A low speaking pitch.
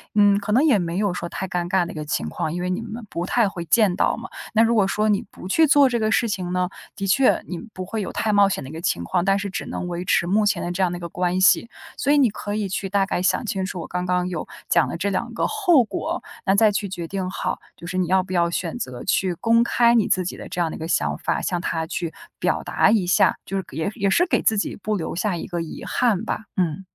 No: high, 190 Hz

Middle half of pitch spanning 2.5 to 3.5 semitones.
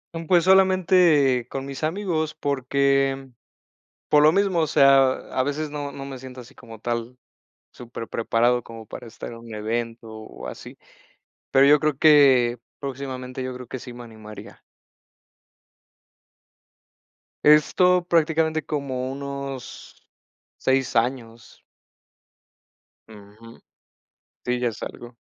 No: average, 3.9 semitones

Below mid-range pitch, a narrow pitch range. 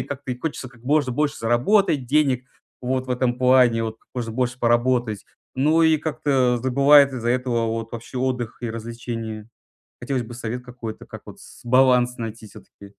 Yes: low, 125 Hz; narrow, 2.1 semitones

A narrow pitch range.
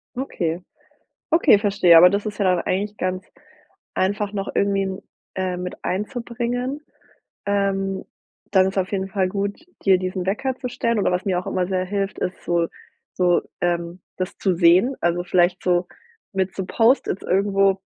Yes: narrow, 2.0 semitones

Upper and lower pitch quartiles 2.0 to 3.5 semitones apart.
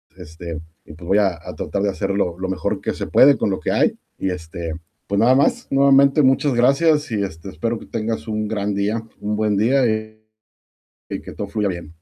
No: average, 4.4 semitones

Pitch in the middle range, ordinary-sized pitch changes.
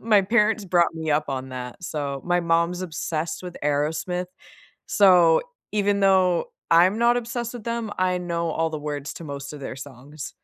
Yes: medium, 170 Hz; average, 4.6 semitones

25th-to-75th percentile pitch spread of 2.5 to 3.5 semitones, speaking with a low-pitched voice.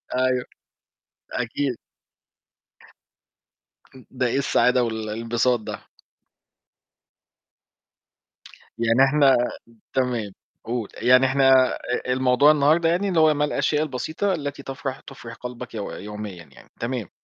Yes: average, 3.2 semitones; low, 130 Hz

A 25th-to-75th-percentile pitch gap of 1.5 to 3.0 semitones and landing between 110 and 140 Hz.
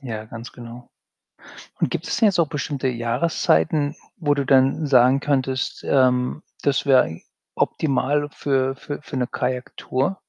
Yes: narrow, 2.5 semitones; low, 135 Hz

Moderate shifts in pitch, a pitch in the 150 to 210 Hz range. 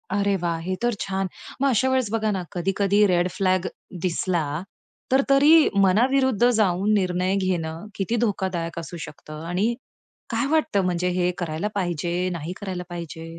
Yes: average, 3.5 semitones; medium, 185 Hz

